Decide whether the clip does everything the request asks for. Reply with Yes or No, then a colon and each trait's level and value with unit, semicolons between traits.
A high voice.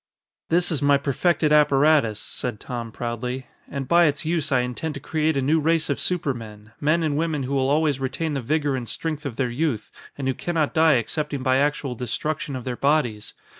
No: medium, 140 Hz